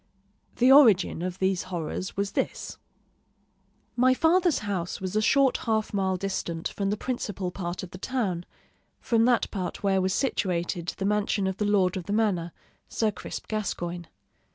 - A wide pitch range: No, average, 3.2 semitones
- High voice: Yes, high, 195 Hz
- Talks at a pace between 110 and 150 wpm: No, average, 165 wpm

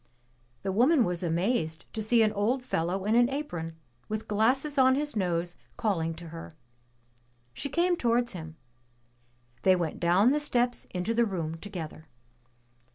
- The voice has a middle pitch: No, high, 205 Hz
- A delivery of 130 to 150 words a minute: No, average, 160 wpm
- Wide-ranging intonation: Yes, wide, 6.4 semitones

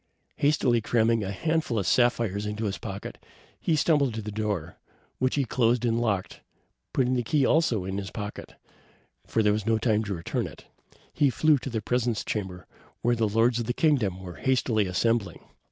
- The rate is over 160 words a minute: Yes, average, 185 wpm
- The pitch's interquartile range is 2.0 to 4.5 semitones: Yes, average, 3.3 semitones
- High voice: No, low, 115 Hz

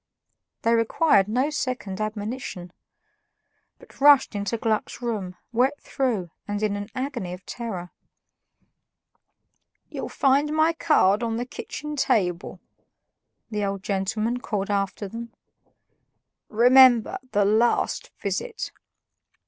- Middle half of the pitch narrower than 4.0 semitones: No, average, 4.3 semitones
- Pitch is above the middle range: Yes, high, 225 Hz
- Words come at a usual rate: No, slow, 110 wpm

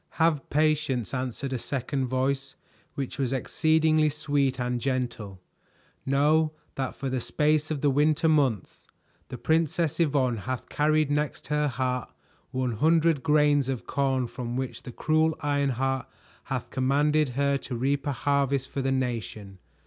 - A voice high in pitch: No, medium, 140 Hz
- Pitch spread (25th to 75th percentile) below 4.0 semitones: Yes, average, 2.7 semitones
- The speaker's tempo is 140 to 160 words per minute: Yes, average, 150 wpm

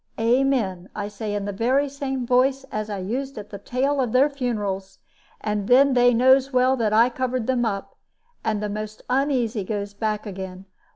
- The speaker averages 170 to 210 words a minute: Yes, average, 185 wpm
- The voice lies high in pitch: Yes, high, 230 Hz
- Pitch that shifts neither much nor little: Yes, average, 4.0 semitones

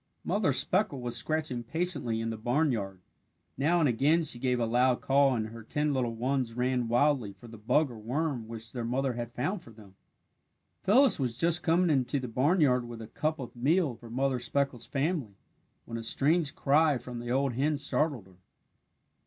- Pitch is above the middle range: No, low, 125 Hz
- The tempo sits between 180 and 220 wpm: Yes, average, 190 wpm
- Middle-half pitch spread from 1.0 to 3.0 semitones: No, average, 4.1 semitones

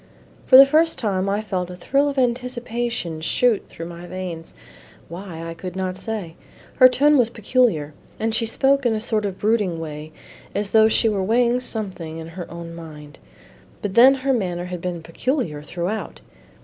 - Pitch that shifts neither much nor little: No, wide, 6.0 semitones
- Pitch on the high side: Yes, high, 200 Hz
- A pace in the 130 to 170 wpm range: No, average, 180 wpm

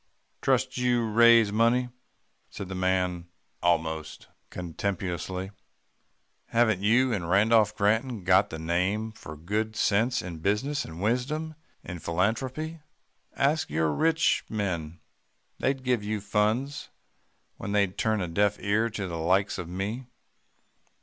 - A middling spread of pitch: Yes, average, 4.6 semitones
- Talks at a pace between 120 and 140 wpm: Yes, slow, 135 wpm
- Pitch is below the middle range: Yes, low, 105 Hz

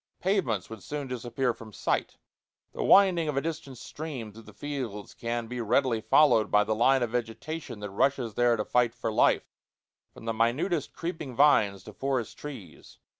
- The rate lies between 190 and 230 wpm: No, average, 175 wpm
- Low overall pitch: Yes, low, 120 Hz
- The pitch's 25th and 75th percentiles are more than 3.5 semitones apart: Yes, average, 4.4 semitones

